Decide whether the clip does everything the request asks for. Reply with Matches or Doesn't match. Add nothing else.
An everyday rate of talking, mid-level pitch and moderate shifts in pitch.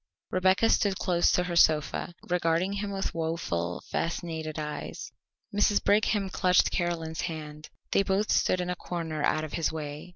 Matches